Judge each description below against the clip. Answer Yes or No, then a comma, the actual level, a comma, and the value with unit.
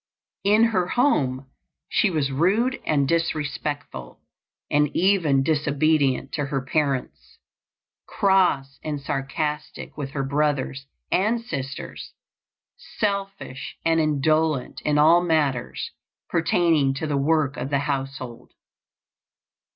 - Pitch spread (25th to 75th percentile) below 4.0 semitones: Yes, average, 3.5 semitones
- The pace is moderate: No, slow, 105 wpm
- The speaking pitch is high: No, medium, 150 Hz